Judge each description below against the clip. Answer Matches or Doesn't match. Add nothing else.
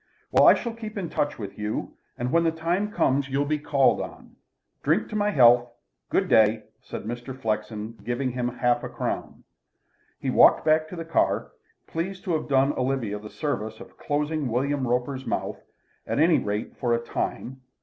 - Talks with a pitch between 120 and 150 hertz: Matches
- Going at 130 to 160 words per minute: Doesn't match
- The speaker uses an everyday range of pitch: Matches